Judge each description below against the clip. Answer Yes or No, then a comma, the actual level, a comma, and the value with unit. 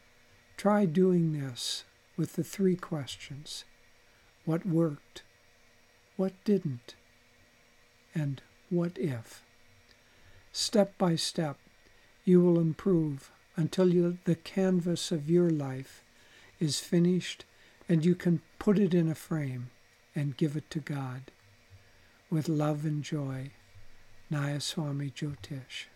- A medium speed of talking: No, slow, 110 wpm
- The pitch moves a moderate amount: No, wide, 6.3 semitones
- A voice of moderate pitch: Yes, medium, 145 Hz